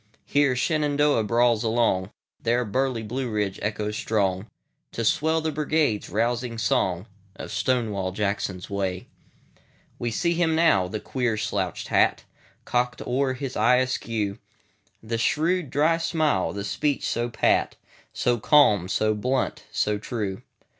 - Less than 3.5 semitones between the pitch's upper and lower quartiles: No, average, 4.6 semitones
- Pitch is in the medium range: No, low, 115 Hz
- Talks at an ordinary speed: No, slow, 115 wpm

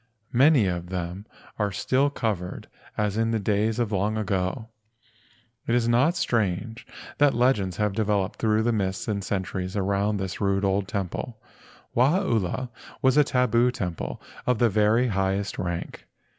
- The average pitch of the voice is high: No, low, 105 Hz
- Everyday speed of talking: Yes, average, 155 wpm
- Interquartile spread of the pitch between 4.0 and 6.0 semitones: No, average, 3.6 semitones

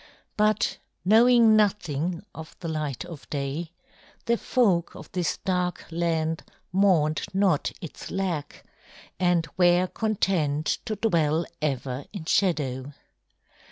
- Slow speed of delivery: Yes, slow, 115 wpm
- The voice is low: No, medium, 170 Hz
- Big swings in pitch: No, average, 4.1 semitones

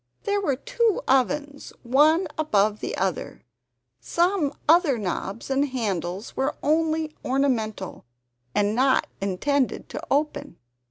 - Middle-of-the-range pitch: No, very high, 275 Hz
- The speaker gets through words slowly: Yes, slow, 115 wpm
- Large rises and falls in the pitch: Yes, wide, 6.3 semitones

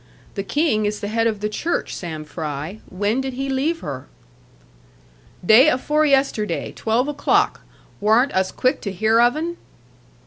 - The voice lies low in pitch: No, high, 225 Hz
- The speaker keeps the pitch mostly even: No, average, 5.1 semitones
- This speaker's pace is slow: No, average, 160 wpm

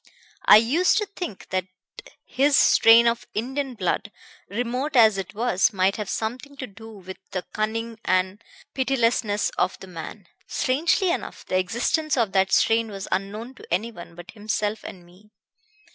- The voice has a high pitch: Yes, high, 220 Hz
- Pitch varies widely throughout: No, average, 4.5 semitones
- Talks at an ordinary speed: Yes, average, 160 wpm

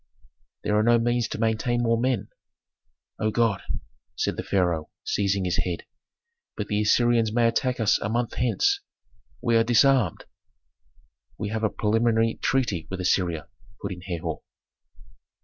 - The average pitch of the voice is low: Yes, low, 110 Hz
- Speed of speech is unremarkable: Yes, average, 150 wpm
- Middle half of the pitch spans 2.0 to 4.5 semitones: Yes, average, 3.6 semitones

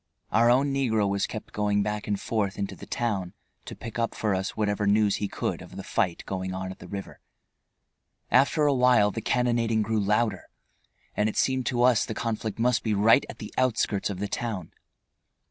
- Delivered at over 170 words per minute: Yes, average, 195 wpm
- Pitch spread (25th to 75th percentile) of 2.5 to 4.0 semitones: Yes, average, 2.8 semitones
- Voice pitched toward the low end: Yes, low, 110 Hz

